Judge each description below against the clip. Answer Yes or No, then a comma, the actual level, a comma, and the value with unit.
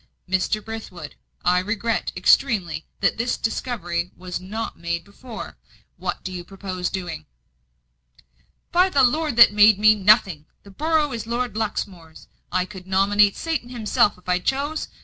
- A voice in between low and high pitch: No, high, 205 Hz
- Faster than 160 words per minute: No, average, 150 wpm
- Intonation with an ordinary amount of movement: Yes, average, 4.4 semitones